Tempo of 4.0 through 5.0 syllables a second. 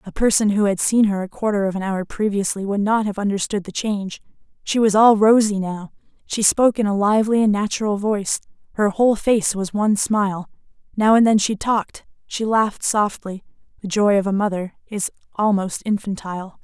No: 5.6 syllables/s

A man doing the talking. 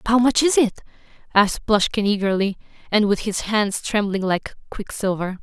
No: female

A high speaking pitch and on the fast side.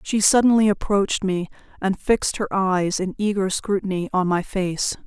No: high, 195 Hz; average, 165 wpm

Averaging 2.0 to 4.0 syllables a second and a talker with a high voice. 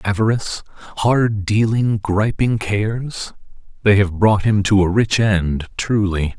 No: 3.9 syllables/s; low, 105 Hz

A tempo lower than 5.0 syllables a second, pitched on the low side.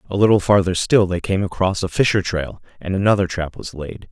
No: 5.6 syllables/s; very low, 95 Hz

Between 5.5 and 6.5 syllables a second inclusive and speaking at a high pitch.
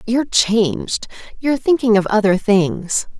No: 4.5 syllables/s; high, 215 Hz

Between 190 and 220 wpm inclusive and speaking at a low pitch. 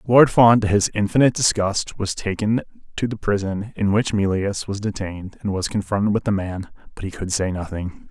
Yes: average, 200 wpm; low, 100 Hz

